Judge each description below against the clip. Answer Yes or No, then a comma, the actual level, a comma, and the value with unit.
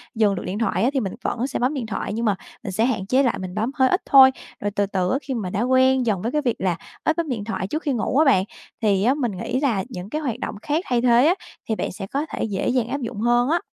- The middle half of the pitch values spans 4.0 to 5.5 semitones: Yes, average, 4.4 semitones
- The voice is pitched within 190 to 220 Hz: No, high, 235 Hz